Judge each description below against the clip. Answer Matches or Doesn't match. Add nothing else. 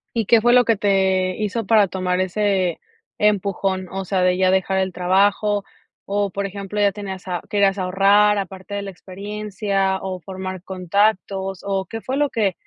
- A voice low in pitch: Doesn't match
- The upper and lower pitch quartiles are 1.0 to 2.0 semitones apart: Matches